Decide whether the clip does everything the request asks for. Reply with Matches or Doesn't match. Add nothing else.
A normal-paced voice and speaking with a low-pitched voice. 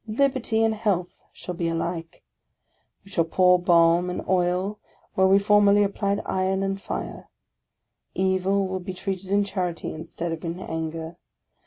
Doesn't match